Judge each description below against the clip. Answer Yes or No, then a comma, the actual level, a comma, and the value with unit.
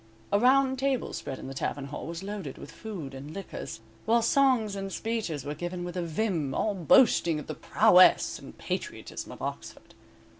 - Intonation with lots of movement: Yes, wide, 6.7 semitones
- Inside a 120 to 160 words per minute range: No, average, 185 wpm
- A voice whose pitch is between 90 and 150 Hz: No, high, 190 Hz